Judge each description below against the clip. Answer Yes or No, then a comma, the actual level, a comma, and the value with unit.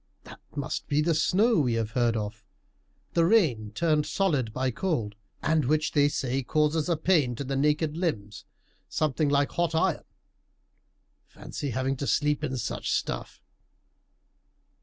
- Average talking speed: Yes, average, 150 wpm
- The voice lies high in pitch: No, medium, 145 Hz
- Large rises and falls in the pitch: No, average, 4.3 semitones